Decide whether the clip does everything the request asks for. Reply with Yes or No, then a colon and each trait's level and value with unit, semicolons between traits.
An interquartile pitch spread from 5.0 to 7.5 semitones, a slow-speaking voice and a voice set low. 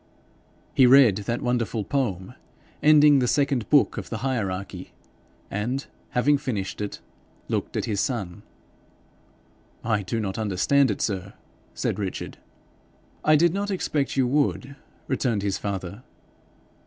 Yes: wide, 5.6 semitones; slow, 130 wpm; low, 120 Hz